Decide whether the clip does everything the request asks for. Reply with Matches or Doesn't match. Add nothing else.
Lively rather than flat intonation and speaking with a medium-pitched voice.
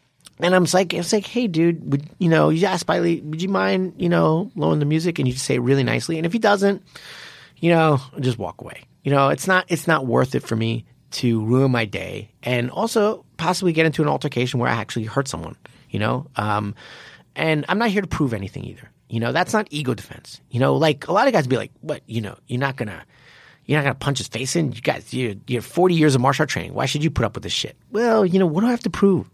Matches